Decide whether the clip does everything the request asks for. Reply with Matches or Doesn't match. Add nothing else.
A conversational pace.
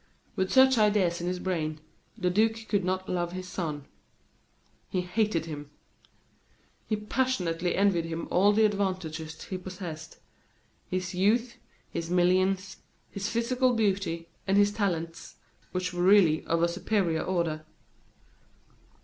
Doesn't match